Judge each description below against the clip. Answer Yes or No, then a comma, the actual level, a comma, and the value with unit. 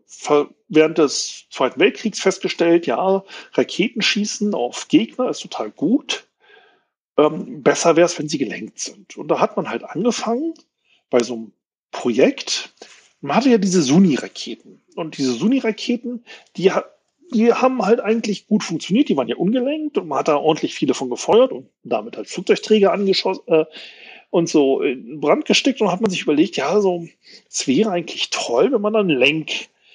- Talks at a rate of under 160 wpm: No, average, 170 wpm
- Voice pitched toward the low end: No, high, 215 Hz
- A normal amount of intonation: No, wide, 6.4 semitones